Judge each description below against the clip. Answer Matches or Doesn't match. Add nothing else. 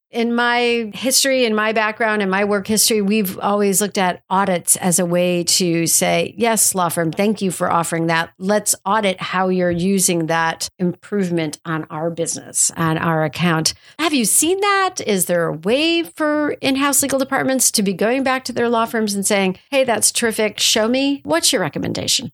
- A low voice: Doesn't match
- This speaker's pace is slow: Doesn't match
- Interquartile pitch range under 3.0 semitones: Doesn't match